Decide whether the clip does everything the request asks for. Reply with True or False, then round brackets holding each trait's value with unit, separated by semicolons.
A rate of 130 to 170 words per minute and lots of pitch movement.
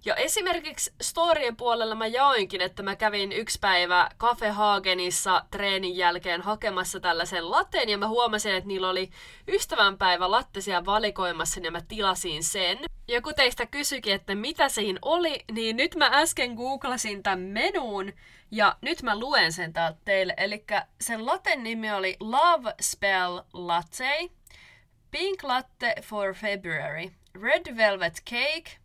True (145 wpm; 5.8 semitones)